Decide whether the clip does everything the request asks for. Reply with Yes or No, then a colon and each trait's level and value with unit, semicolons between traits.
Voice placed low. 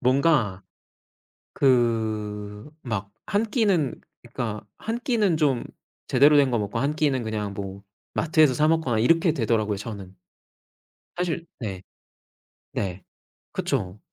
Yes: low, 120 Hz